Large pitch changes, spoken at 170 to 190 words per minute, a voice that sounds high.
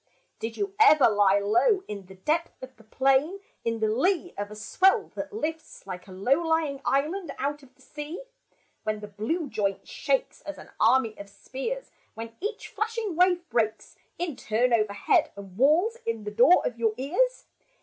Yes: wide, 8.5 semitones; average, 185 wpm; very high, 265 Hz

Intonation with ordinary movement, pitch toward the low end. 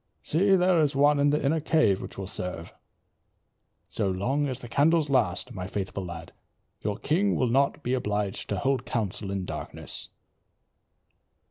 No: wide, 6.9 semitones; low, 130 Hz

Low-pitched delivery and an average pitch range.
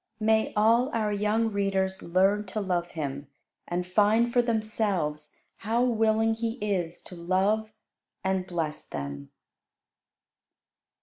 No: high, 200 Hz; average, 3.9 semitones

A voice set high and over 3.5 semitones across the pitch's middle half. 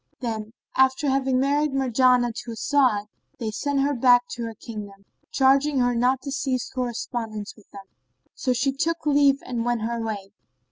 No: very high, 250 Hz; average, 3.2 semitones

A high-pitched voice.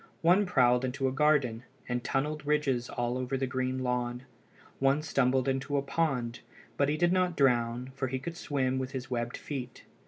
No: low, 130 Hz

